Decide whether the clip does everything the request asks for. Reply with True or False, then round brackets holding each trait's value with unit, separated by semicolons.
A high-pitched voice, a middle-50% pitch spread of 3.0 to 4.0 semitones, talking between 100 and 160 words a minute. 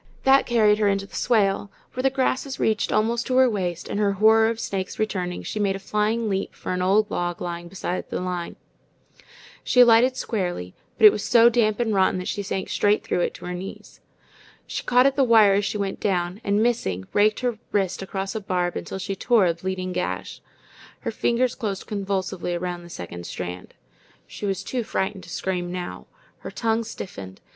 False (200 Hz; 3.5 semitones; 205 wpm)